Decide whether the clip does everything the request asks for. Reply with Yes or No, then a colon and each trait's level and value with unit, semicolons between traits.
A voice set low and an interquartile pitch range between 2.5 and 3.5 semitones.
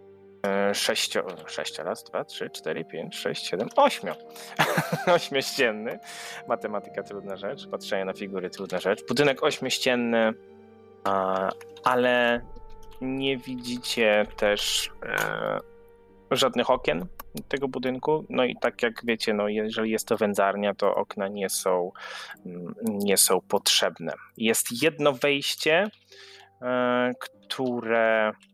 No: low, 110 Hz; average, 4.7 semitones